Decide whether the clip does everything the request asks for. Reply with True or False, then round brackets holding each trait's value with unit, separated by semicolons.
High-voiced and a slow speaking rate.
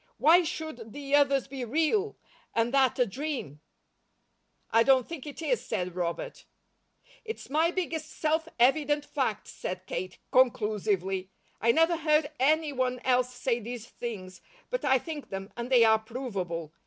False (255 Hz; 155 wpm)